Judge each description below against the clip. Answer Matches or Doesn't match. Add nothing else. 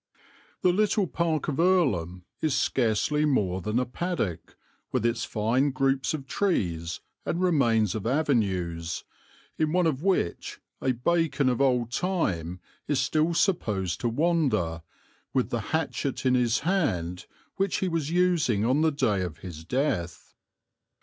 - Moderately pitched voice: Doesn't match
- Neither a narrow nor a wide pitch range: Doesn't match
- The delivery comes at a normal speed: Matches